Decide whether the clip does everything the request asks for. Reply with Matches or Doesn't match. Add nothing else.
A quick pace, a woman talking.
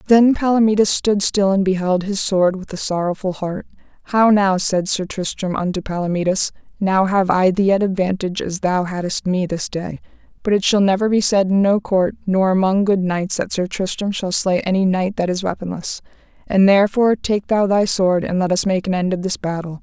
Matches